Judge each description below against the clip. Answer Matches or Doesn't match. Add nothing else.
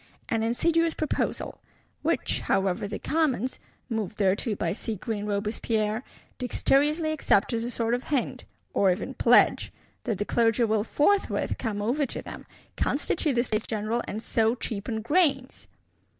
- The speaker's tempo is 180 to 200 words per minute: Doesn't match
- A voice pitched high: Matches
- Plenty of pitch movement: Doesn't match